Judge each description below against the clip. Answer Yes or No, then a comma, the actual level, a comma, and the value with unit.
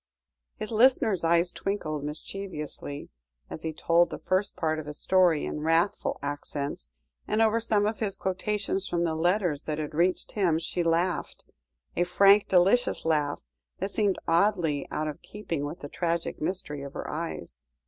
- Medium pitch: Yes, medium, 170 Hz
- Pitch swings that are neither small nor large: Yes, average, 4.3 semitones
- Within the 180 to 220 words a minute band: No, average, 165 wpm